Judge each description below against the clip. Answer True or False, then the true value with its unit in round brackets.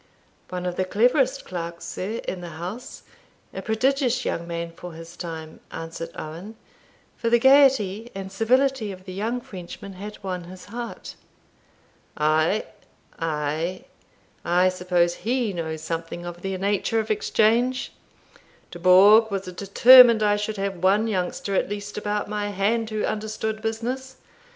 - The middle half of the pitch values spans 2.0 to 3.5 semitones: False (4.2 semitones)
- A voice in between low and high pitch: False (200 Hz)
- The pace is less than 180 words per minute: True (145 wpm)